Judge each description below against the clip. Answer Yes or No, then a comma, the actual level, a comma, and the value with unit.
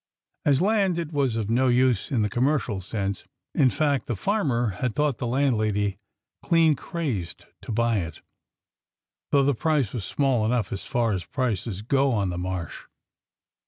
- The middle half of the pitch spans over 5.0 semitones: Yes, wide, 5.4 semitones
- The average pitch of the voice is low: Yes, low, 120 Hz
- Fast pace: No, average, 170 wpm